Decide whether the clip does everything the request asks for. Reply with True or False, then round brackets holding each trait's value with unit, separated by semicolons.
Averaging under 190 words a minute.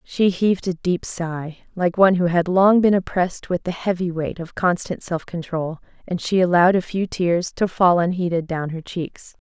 False (205 wpm)